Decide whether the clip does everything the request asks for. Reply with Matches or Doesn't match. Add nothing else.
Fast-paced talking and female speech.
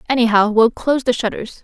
Doesn't match